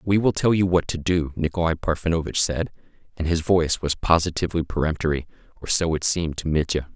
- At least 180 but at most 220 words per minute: Yes, average, 190 wpm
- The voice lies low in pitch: Yes, very low, 80 Hz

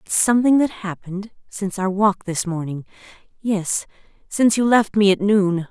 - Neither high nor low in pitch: No, high, 200 Hz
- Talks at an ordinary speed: Yes, average, 160 wpm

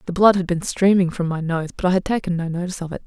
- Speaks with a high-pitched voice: No, medium, 180 Hz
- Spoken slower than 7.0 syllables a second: No, 7.1 syllables/s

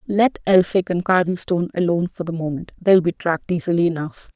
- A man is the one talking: No, female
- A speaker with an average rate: Yes, average, 165 wpm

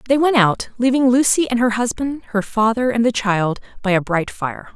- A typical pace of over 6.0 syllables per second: No, 5.0 syllables/s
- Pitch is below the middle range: No, high, 230 Hz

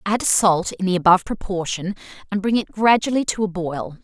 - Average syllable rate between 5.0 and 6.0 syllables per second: Yes, 5.3 syllables/s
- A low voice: No, high, 195 Hz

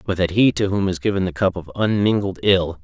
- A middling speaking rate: No, fast, 255 wpm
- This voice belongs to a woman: No, male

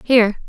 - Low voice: No, high, 225 Hz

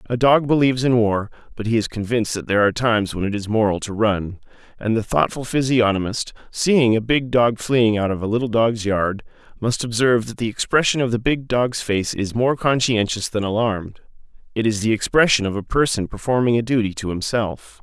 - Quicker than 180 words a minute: Yes, fast, 205 wpm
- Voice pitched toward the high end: No, low, 115 Hz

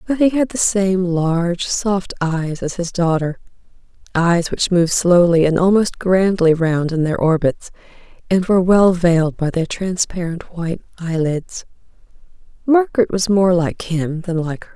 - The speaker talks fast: No, average, 160 wpm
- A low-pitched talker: No, medium, 180 Hz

